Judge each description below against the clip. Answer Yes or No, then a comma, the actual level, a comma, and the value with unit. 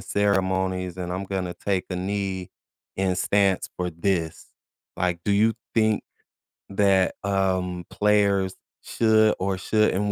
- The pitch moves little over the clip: Yes, narrow, 1.7 semitones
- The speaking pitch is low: Yes, very low, 95 Hz